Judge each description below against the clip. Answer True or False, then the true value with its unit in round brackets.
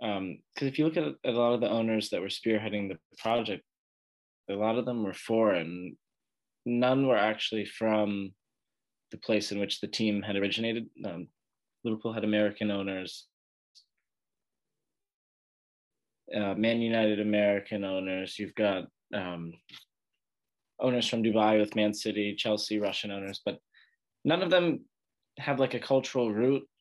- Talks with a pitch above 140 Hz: False (105 Hz)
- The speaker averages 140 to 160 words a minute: True (150 wpm)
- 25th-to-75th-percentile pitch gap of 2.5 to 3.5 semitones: True (3.0 semitones)